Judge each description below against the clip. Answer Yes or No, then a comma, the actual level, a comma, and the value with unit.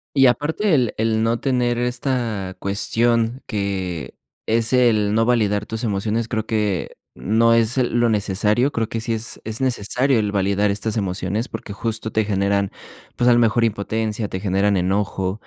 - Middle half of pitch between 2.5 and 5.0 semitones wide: Yes, average, 2.8 semitones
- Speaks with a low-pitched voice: Yes, low, 110 Hz